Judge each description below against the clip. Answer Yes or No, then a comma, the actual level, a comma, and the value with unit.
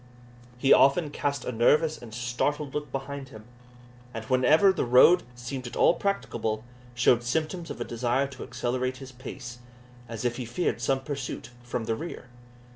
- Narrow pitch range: No, average, 3.0 semitones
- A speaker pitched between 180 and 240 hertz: No, low, 130 Hz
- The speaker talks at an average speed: Yes, average, 170 wpm